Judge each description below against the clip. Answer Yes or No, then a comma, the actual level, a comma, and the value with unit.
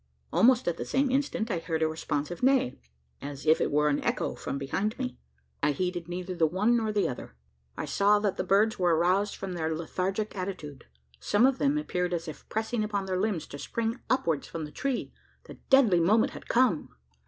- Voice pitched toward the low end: No, medium, 185 Hz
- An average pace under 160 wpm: No, fast, 205 wpm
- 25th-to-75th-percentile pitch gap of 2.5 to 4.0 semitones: No, average, 5.3 semitones